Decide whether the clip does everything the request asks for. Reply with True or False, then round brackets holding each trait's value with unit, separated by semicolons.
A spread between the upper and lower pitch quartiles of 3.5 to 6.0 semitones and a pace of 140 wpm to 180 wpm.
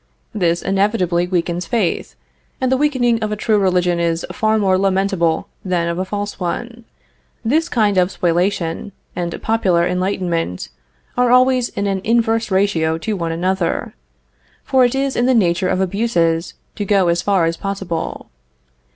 True (4.4 semitones; 160 wpm)